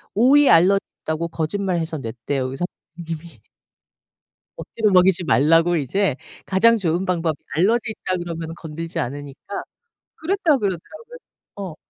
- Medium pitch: Yes, medium, 175 Hz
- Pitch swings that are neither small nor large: Yes, average, 4.0 semitones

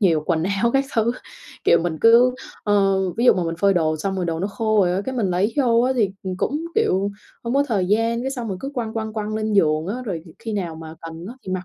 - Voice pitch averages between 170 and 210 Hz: Yes, high, 205 Hz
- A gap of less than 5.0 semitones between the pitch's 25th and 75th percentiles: Yes, average, 4.6 semitones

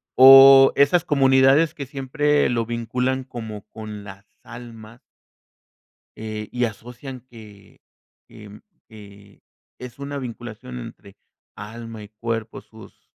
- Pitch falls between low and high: No, low, 120 Hz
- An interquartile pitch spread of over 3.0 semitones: Yes, average, 3.5 semitones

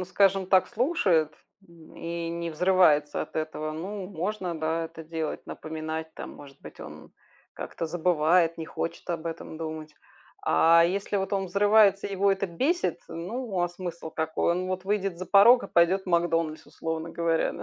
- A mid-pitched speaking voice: Yes, medium, 170 Hz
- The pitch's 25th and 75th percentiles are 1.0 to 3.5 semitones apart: Yes, average, 3.1 semitones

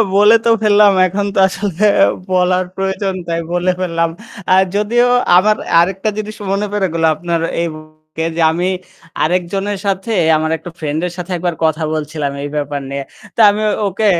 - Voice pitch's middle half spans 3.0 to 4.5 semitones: Yes, average, 3.6 semitones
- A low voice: No, medium, 180 Hz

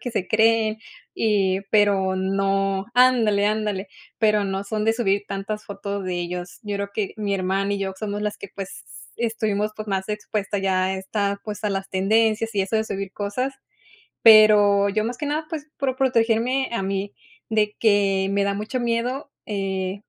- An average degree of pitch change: No, narrow, 2.1 semitones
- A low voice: No, high, 205 Hz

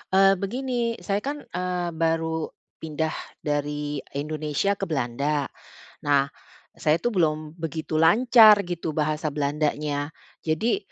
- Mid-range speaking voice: Yes, medium, 155 Hz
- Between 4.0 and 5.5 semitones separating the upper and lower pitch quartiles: No, average, 3.5 semitones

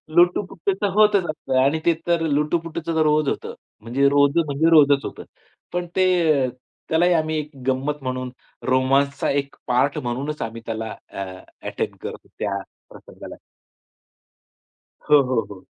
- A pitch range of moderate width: Yes, average, 4.0 semitones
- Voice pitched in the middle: Yes, medium, 145 Hz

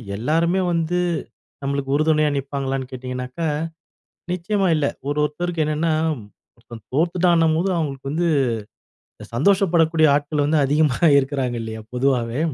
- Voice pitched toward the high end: No, medium, 150 Hz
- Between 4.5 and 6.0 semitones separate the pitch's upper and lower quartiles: No, average, 3.7 semitones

